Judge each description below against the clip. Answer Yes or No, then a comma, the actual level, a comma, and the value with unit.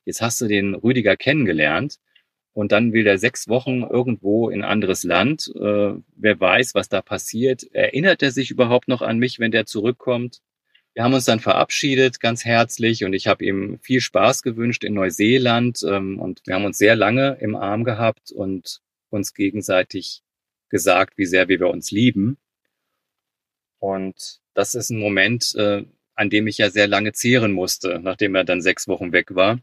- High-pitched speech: No, low, 110 Hz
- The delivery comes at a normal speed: Yes, average, 180 wpm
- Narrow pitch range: No, average, 3.6 semitones